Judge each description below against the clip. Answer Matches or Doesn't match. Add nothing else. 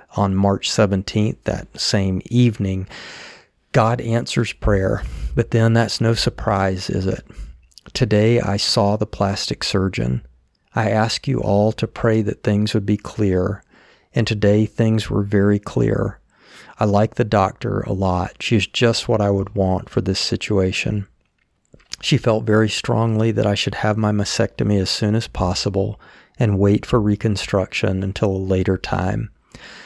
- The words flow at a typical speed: Matches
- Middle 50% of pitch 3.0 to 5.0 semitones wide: Doesn't match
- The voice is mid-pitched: Doesn't match